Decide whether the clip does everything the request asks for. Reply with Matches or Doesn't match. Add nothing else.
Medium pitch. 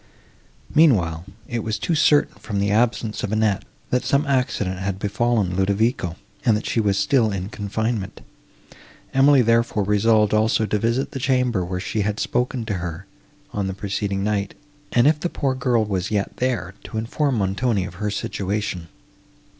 Doesn't match